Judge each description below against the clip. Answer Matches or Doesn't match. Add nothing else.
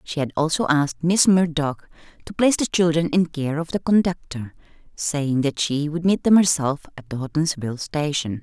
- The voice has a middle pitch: Matches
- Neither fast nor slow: Matches